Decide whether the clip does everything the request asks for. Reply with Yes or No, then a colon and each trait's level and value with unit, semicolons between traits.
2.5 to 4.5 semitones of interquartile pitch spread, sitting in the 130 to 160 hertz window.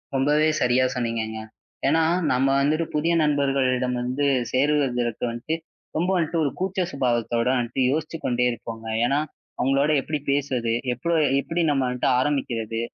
Yes: average, 3.5 semitones; low, 135 Hz